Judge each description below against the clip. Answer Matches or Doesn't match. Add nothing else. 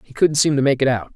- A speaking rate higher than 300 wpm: Matches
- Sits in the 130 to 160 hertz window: Matches